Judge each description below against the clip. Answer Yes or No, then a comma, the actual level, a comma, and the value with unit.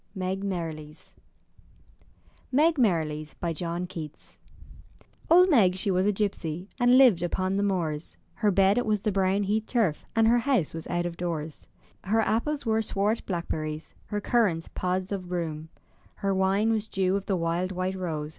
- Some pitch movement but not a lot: Yes, average, 4.0 semitones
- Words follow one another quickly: No, average, 175 wpm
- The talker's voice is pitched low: No, high, 190 Hz